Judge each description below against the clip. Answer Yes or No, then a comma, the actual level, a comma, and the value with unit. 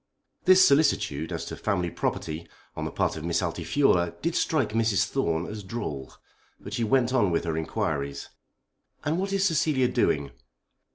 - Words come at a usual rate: Yes, average, 165 wpm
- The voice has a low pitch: Yes, low, 105 Hz